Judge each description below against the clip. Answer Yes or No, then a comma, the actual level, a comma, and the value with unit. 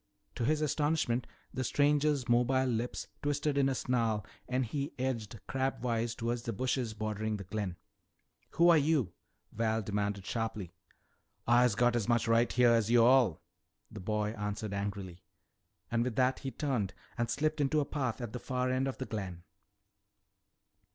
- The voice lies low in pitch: Yes, low, 120 Hz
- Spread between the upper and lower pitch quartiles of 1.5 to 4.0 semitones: Yes, average, 3.5 semitones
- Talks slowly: No, average, 165 wpm